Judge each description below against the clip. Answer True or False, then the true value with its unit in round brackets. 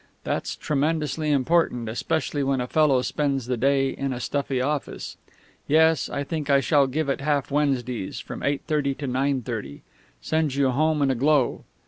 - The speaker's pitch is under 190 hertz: True (140 Hz)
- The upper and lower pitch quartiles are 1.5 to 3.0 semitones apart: True (2.4 semitones)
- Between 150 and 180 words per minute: True (175 wpm)